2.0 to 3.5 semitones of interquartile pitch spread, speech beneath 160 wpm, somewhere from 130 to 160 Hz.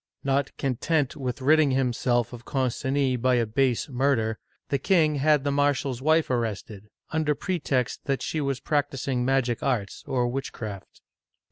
Yes: average, 2.7 semitones; average, 145 wpm; low, 135 Hz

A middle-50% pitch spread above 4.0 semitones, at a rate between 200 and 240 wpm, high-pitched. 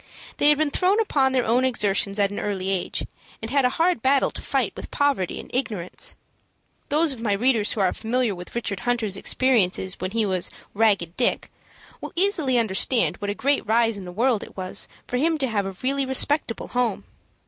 Yes: average, 5.1 semitones; fast, 205 wpm; high, 230 Hz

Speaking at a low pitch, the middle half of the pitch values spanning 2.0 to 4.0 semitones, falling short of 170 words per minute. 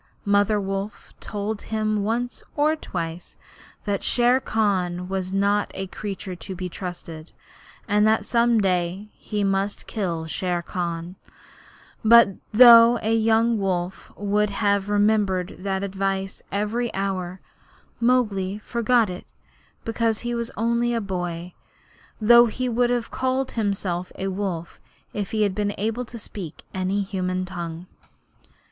No: high, 200 Hz; average, 3.4 semitones; average, 140 wpm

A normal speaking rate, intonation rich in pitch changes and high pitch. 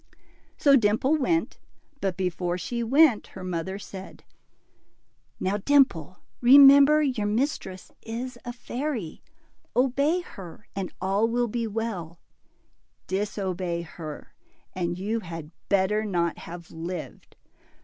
No: slow, 115 wpm; wide, 5.7 semitones; high, 205 Hz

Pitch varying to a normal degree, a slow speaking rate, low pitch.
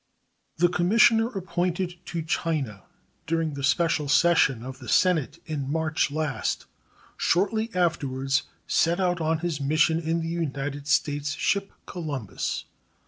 No: average, 3.5 semitones; slow, 130 wpm; medium, 160 Hz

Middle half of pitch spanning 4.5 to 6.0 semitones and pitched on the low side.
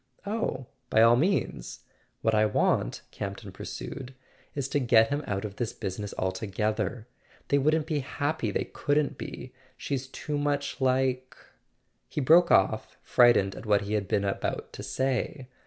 Yes: average, 5.1 semitones; low, 130 Hz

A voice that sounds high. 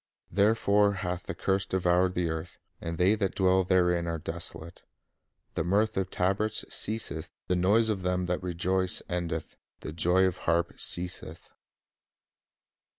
No: very low, 90 Hz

